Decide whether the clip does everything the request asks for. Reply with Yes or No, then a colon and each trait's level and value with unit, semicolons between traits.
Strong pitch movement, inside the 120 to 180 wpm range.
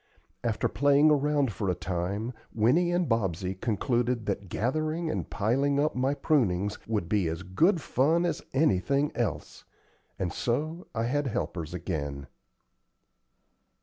Yes: wide, 7.3 semitones; slow, 135 wpm